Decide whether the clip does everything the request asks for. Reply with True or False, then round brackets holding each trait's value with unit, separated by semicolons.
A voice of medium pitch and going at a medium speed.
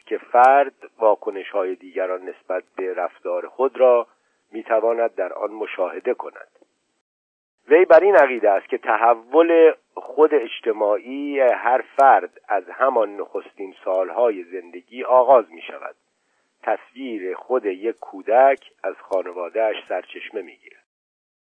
True (165 Hz; 125 wpm)